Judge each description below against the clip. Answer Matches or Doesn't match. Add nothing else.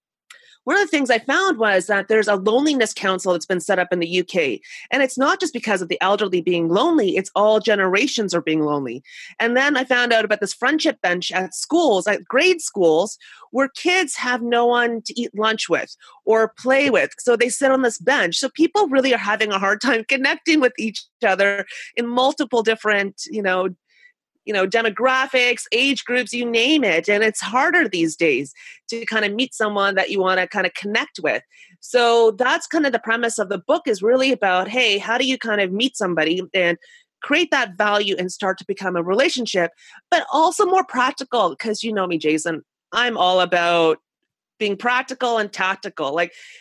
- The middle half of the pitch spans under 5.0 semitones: Doesn't match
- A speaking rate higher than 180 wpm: Matches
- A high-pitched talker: Matches